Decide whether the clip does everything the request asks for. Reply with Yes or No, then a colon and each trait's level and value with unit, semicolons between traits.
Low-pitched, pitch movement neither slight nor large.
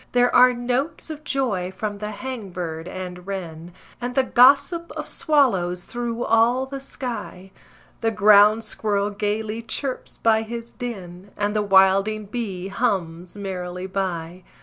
No: high, 210 Hz; average, 4.5 semitones